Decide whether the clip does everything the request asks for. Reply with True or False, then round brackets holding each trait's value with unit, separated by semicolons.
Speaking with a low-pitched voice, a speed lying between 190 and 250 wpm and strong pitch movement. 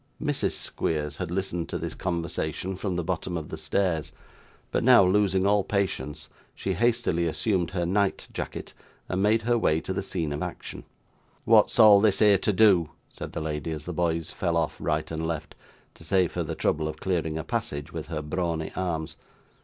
False (85 Hz; 195 wpm; 3.4 semitones)